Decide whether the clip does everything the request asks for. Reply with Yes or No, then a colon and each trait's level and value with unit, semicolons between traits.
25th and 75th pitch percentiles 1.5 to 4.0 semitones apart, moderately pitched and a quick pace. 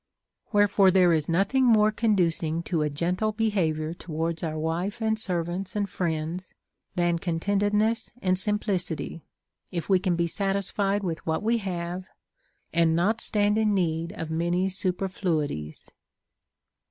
No: average, 3.6 semitones; medium, 180 Hz; average, 140 wpm